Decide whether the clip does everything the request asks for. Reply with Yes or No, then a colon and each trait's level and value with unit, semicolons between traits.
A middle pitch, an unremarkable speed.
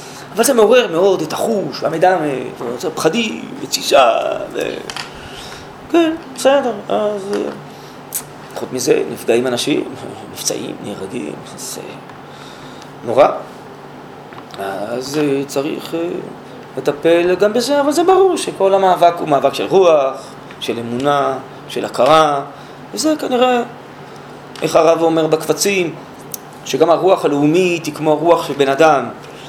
Yes: medium, 165 Hz; average, 110 wpm